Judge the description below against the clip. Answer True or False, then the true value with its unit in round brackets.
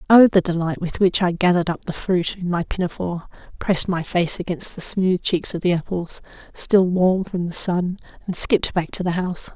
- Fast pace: True (215 wpm)